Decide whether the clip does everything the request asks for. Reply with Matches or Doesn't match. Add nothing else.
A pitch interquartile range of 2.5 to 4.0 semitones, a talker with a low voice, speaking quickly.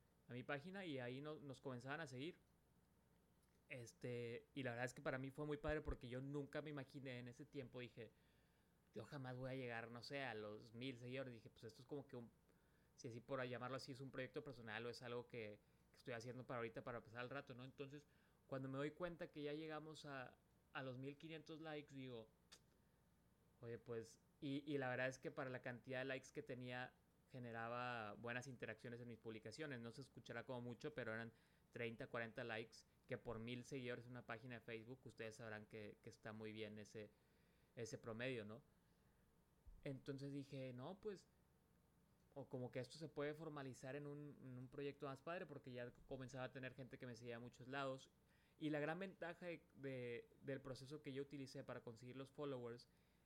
Matches